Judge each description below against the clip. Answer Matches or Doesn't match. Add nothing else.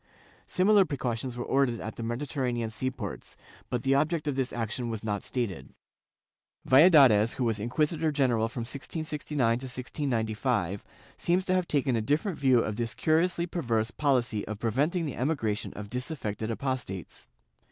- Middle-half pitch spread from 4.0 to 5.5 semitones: Matches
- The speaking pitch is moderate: Doesn't match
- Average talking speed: Matches